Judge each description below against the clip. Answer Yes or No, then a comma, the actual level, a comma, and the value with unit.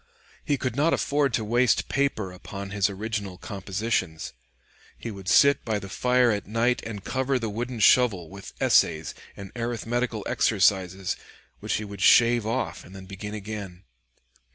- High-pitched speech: No, low, 105 Hz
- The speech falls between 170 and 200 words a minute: No, average, 155 wpm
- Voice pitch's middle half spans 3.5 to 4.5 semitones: Yes, average, 3.8 semitones